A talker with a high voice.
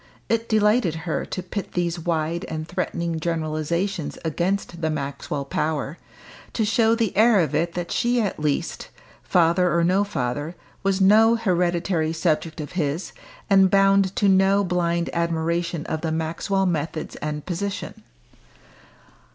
No: medium, 170 Hz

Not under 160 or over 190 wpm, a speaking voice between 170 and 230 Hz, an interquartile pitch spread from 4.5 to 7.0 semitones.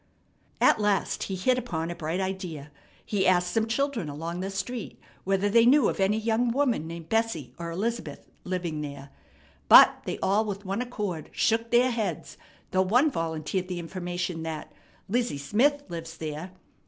Yes: average, 165 wpm; high, 190 Hz; wide, 5.4 semitones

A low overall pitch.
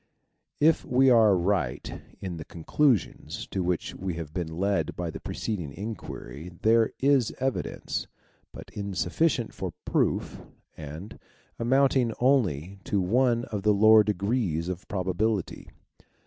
Yes: low, 100 Hz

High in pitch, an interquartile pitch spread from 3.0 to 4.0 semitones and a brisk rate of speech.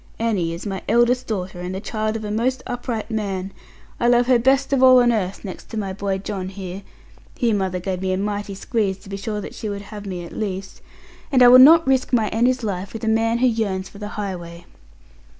Yes: high, 210 Hz; average, 3.7 semitones; fast, 235 wpm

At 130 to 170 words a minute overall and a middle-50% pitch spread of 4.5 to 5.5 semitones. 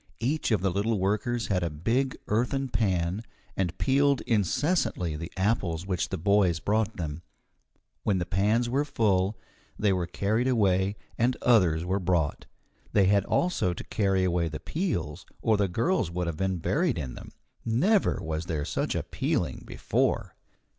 Yes: average, 165 wpm; average, 4.9 semitones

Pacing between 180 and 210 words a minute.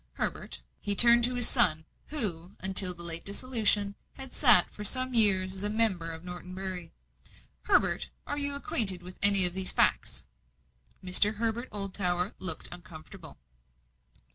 No: average, 145 wpm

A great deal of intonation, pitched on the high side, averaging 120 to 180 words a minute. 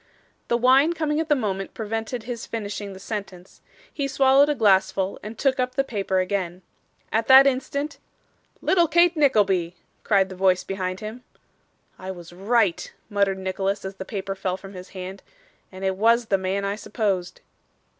No: average, 5.0 semitones; high, 200 Hz; average, 170 wpm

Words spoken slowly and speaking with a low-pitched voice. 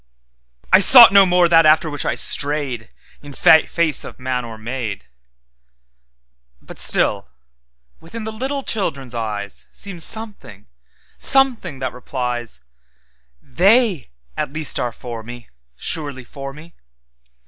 Yes: slow, 110 wpm; low, 130 Hz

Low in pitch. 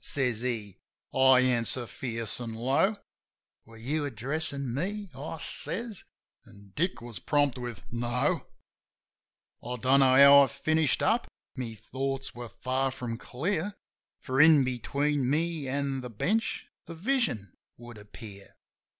Yes: low, 130 Hz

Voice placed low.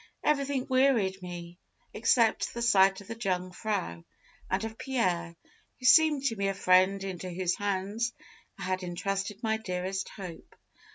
No: high, 195 Hz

